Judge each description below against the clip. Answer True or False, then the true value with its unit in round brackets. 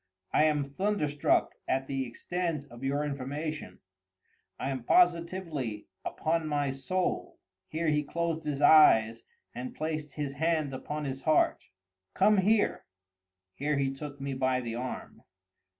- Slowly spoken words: True (130 wpm)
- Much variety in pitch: False (3.2 semitones)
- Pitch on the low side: False (145 Hz)